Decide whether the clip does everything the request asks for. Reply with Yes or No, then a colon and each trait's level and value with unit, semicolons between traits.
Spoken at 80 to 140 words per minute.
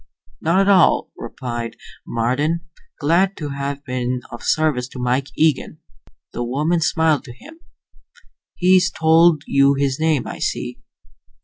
Yes: slow, 135 wpm